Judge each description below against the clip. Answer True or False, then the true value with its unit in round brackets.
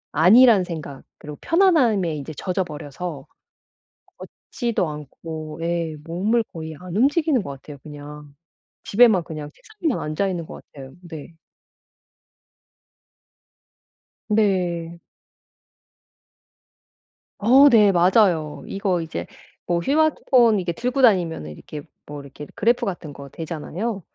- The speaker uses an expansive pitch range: True (6.3 semitones)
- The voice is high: False (175 Hz)